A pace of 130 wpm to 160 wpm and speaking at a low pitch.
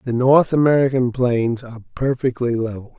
Yes: average, 140 wpm; low, 125 Hz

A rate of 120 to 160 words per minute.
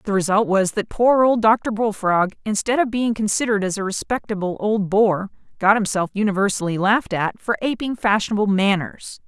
No: average, 170 wpm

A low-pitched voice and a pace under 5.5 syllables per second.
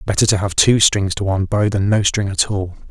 No: low, 100 Hz; 5.6 syllables/s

